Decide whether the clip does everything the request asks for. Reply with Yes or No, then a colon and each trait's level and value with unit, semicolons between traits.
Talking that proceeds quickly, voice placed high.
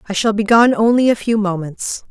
Yes: fast, 230 wpm; high, 210 Hz